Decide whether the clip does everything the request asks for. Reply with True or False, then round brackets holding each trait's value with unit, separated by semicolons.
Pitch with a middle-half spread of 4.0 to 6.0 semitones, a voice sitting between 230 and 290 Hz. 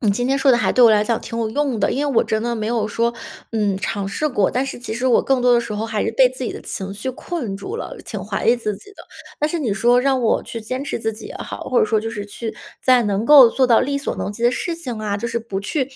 False (3.2 semitones; 235 Hz)